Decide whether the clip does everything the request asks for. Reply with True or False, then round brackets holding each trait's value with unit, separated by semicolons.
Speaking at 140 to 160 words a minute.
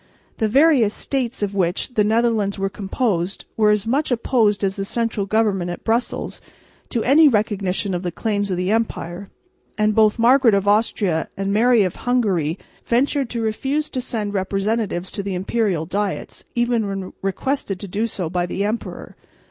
False (170 wpm)